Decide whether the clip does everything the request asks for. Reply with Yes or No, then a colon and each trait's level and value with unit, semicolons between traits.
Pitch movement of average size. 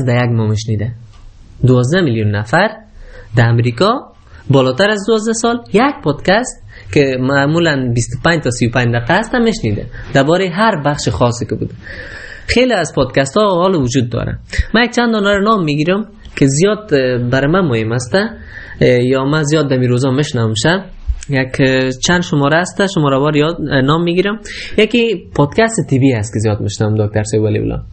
No: wide, 7.2 semitones